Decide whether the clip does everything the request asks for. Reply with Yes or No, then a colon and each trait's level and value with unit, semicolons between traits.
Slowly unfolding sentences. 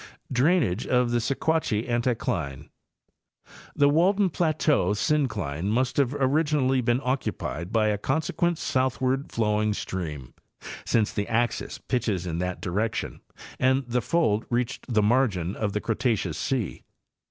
Yes: slow, 130 wpm